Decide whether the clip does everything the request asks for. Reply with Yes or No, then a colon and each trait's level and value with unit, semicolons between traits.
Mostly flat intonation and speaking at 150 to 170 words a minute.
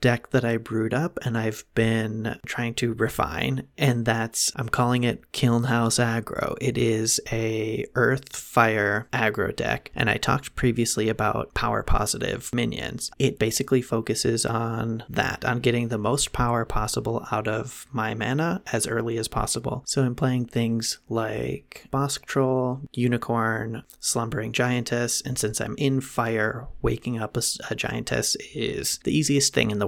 Yes: narrow, 2.0 semitones; average, 160 wpm